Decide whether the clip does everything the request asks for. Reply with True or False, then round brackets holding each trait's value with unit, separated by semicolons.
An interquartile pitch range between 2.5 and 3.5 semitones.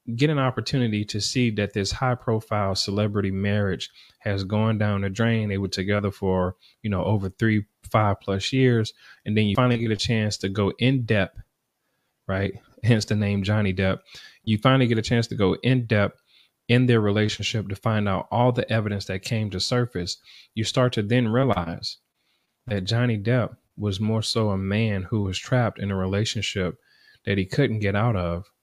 True (2.8 semitones)